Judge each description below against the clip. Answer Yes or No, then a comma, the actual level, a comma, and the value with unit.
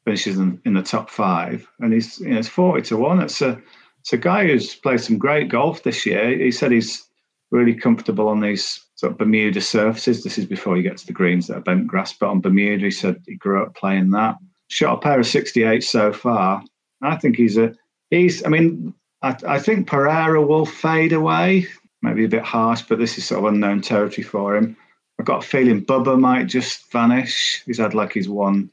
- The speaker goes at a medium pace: No, fast, 215 wpm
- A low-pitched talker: Yes, low, 115 Hz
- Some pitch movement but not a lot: No, wide, 6.7 semitones